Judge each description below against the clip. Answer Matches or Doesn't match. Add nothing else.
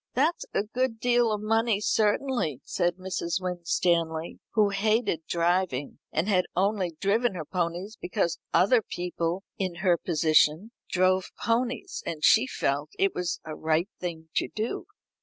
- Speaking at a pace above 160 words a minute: Doesn't match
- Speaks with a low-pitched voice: Doesn't match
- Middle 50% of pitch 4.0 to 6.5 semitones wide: Matches